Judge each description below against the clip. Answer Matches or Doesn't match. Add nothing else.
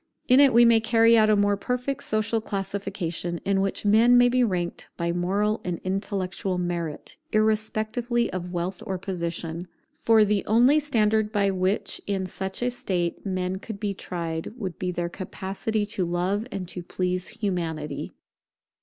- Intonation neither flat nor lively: Matches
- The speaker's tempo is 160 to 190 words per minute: Matches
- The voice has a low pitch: Doesn't match